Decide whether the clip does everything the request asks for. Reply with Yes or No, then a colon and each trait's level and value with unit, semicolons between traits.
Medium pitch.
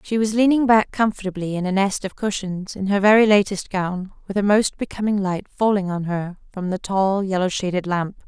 No: high, 195 Hz